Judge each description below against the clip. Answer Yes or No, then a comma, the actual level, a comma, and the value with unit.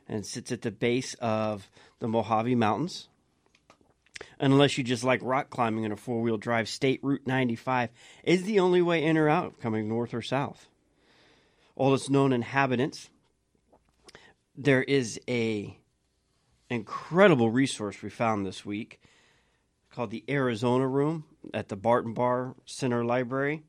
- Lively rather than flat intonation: No, average, 3.2 semitones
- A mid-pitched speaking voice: No, low, 125 Hz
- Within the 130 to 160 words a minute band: Yes, average, 140 wpm